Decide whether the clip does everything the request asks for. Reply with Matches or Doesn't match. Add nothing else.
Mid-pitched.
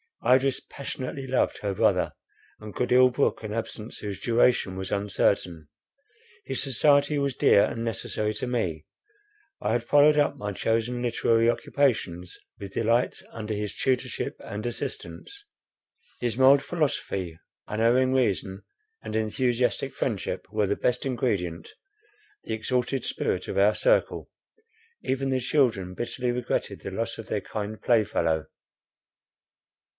Doesn't match